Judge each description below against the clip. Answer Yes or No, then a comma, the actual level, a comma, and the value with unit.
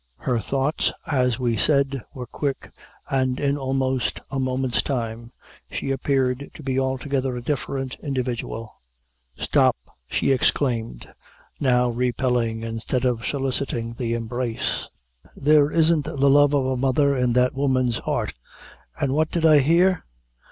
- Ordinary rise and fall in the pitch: No, narrow, 2.2 semitones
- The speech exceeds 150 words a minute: No, slow, 135 wpm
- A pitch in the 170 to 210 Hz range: No, low, 130 Hz